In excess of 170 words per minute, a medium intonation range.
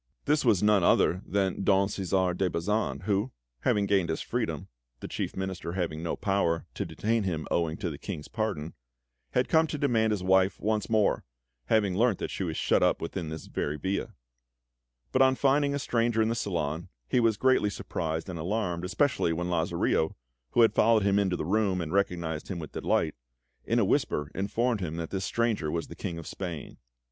Yes: average, 195 wpm; average, 4.5 semitones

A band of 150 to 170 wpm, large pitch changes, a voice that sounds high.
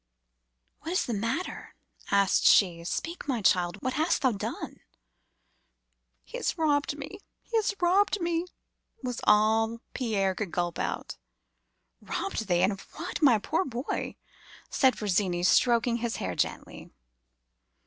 No: average, 140 wpm; wide, 8.0 semitones; high, 235 Hz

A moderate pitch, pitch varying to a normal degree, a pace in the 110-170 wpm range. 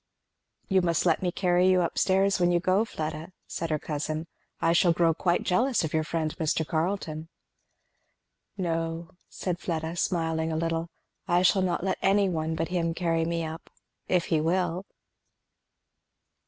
No: medium, 170 Hz; narrow, 2.1 semitones; average, 165 wpm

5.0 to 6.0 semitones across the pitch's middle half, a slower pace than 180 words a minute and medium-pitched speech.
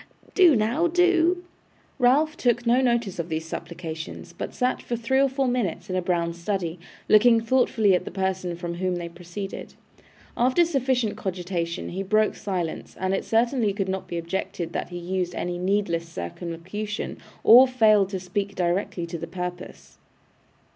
No: wide, 5.5 semitones; average, 165 wpm; high, 195 Hz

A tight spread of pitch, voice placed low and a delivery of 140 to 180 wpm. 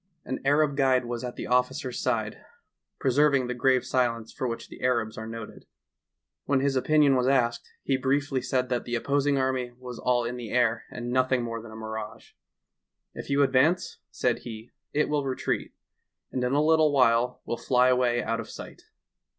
No: narrow, 2.3 semitones; low, 125 Hz; average, 190 wpm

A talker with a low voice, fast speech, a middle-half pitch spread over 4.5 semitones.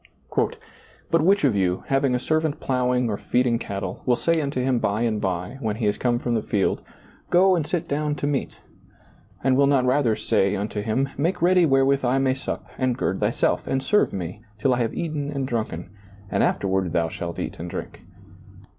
Yes: low, 125 Hz; fast, 210 wpm; average, 5.1 semitones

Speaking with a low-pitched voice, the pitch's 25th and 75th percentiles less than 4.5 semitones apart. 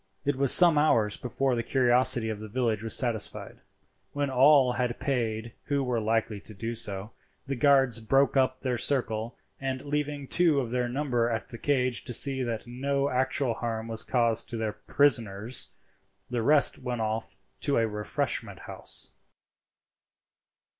Yes: low, 125 Hz; average, 3.3 semitones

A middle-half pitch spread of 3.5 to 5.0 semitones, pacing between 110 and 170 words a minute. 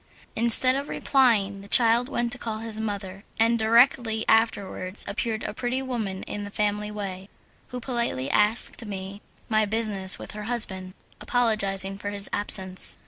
No: average, 2.9 semitones; average, 155 wpm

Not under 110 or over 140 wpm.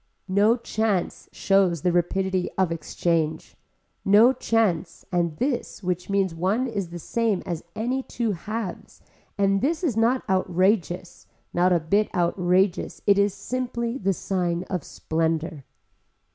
Yes: slow, 135 wpm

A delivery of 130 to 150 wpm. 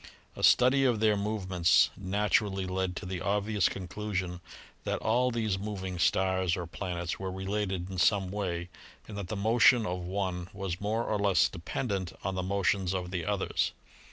No: average, 175 wpm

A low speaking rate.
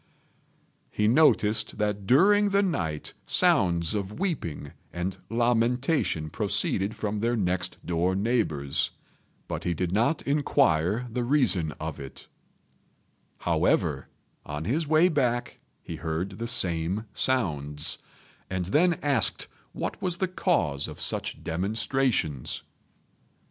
Yes: slow, 115 wpm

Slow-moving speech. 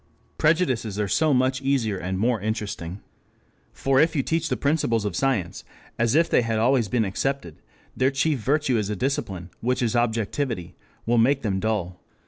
No: average, 175 wpm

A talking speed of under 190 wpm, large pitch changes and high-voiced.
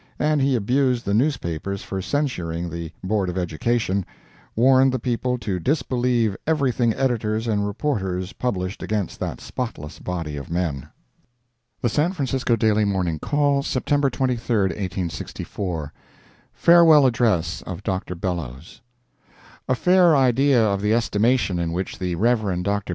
No: slow, 135 wpm; wide, 6.0 semitones; low, 110 Hz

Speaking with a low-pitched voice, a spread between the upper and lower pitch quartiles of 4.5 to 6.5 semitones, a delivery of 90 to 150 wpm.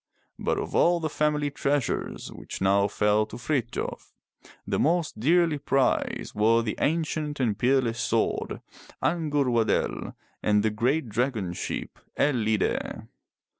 Yes: low, 125 Hz; wide, 5.4 semitones; average, 140 wpm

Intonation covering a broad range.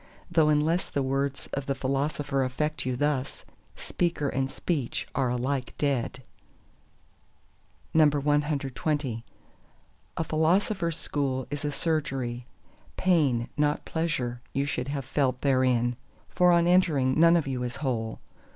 No: average, 3.1 semitones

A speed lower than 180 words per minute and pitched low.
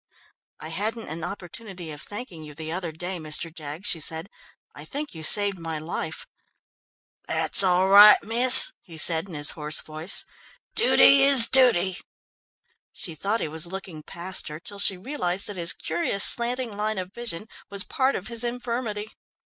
No: average, 170 wpm; high, 190 Hz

